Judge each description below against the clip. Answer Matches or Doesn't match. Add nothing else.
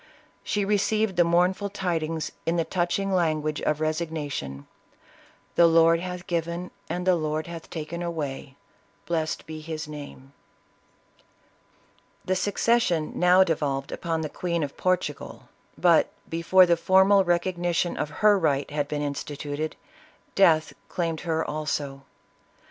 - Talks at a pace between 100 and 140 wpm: Matches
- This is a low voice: Doesn't match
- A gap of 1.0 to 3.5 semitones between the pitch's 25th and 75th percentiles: Matches